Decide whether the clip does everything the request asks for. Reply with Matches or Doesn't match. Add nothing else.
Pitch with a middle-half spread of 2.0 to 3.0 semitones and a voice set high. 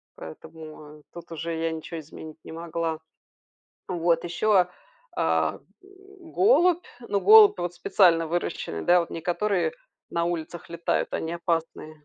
Doesn't match